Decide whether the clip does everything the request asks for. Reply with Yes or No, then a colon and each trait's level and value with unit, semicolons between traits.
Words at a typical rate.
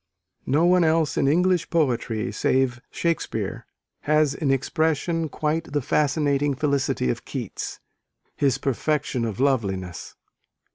No: slow, 115 wpm